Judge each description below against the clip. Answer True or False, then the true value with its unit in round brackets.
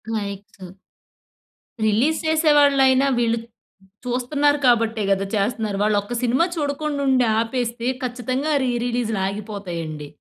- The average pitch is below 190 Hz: False (240 Hz)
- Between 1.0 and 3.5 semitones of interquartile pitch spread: False (4.4 semitones)